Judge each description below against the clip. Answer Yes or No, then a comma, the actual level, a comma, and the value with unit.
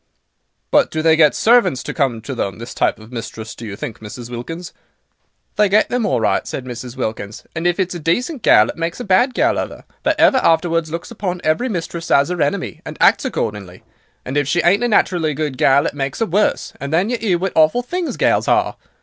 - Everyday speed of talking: No, fast, 235 wpm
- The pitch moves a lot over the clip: Yes, wide, 7.0 semitones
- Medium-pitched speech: Yes, medium, 160 Hz